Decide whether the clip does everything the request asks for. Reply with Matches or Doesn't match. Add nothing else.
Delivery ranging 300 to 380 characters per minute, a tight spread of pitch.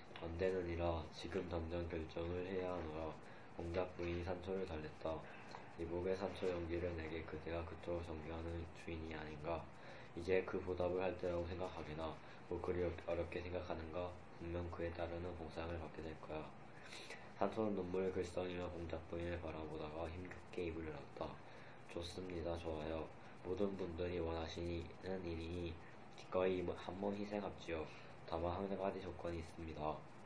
Matches